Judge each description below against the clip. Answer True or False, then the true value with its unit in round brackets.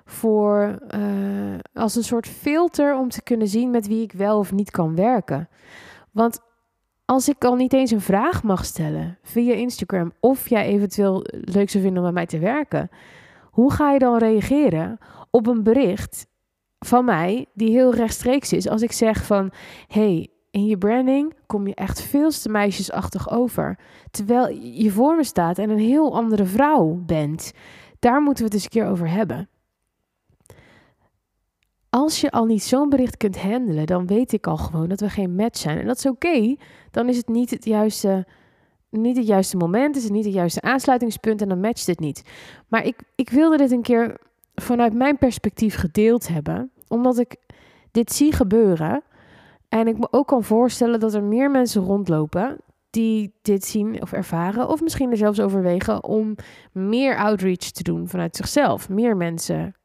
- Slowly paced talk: False (180 wpm)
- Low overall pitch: False (220 Hz)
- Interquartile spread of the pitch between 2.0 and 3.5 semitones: False (4.0 semitones)